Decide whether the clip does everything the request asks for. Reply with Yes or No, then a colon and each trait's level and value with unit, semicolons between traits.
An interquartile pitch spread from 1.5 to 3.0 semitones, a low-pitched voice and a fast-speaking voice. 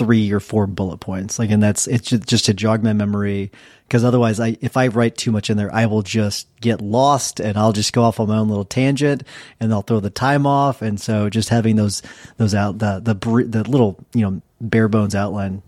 Yes: narrow, 2.4 semitones; low, 110 Hz; fast, 235 wpm